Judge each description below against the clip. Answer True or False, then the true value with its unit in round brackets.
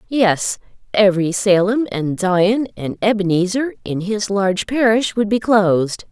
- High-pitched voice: True (205 Hz)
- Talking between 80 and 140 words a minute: True (135 wpm)